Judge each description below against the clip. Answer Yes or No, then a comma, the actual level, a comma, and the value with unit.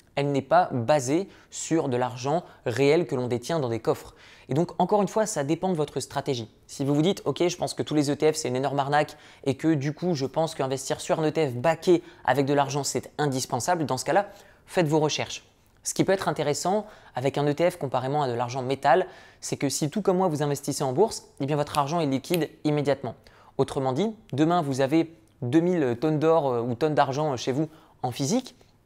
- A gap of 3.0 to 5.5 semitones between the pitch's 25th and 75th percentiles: Yes, average, 3.6 semitones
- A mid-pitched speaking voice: Yes, medium, 145 Hz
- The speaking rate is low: No, fast, 220 wpm